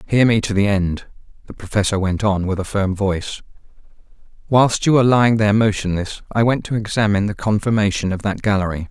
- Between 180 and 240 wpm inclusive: Yes, average, 190 wpm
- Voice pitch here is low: Yes, low, 105 Hz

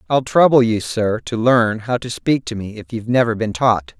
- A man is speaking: Yes, male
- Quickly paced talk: Yes, fast, 240 wpm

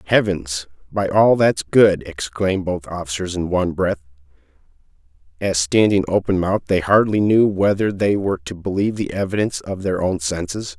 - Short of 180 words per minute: Yes, average, 160 wpm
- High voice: No, very low, 95 Hz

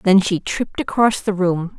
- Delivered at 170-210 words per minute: Yes, average, 200 wpm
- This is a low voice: No, high, 190 Hz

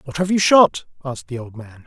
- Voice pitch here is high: No, medium, 145 Hz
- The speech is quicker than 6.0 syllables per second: No, 5.7 syllables/s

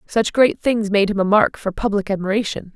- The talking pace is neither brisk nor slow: No, fast, 215 wpm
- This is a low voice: No, high, 205 Hz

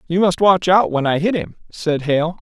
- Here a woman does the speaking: No, male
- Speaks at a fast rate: Yes, fast, 245 wpm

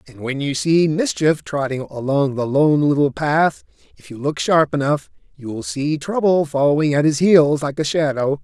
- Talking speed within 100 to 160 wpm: No, average, 185 wpm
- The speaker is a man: Yes, male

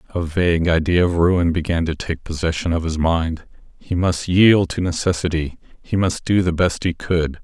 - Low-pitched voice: Yes, very low, 85 Hz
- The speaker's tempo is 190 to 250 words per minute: Yes, average, 195 wpm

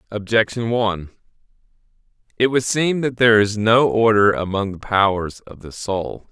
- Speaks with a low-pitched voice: Yes, low, 105 Hz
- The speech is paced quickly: No, average, 150 wpm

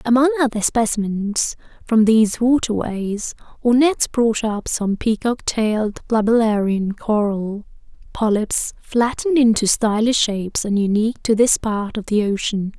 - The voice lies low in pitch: No, high, 220 Hz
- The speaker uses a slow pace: Yes, slow, 130 wpm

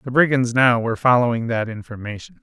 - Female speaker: No, male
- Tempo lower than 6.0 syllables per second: No, 6.1 syllables/s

